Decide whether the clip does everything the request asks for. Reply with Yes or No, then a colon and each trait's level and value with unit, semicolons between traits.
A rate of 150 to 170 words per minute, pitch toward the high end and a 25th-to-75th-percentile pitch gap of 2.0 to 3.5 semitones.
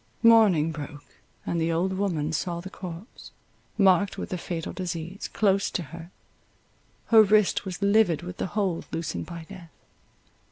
No: average, 155 wpm; medium, 180 Hz; average, 3.2 semitones